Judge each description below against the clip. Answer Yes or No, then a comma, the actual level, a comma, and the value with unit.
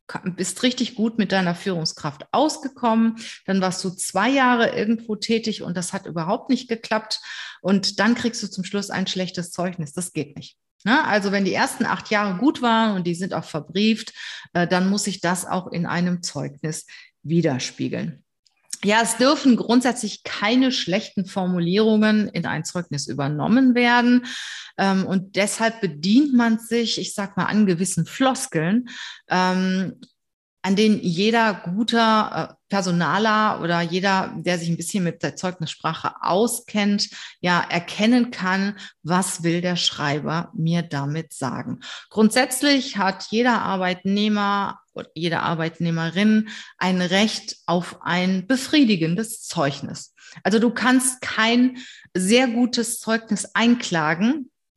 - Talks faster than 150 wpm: No, average, 135 wpm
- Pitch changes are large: No, average, 4.4 semitones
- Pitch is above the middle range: Yes, high, 195 Hz